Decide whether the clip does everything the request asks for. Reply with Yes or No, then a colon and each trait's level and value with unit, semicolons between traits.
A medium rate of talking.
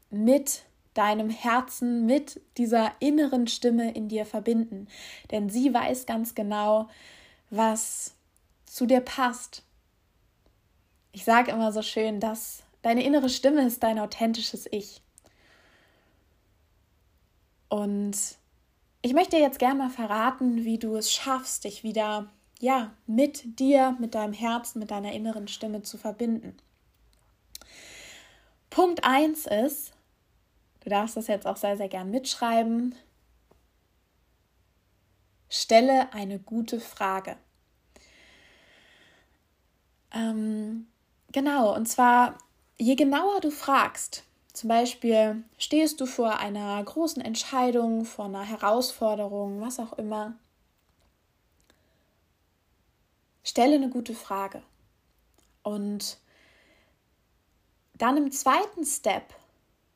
No: slow, 105 wpm